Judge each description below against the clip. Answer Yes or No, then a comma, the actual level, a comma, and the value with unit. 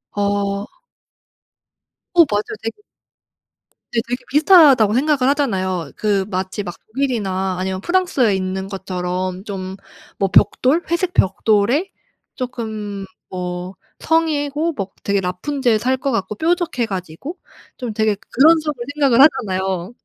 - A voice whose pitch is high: Yes, high, 215 Hz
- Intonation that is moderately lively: No, wide, 6.7 semitones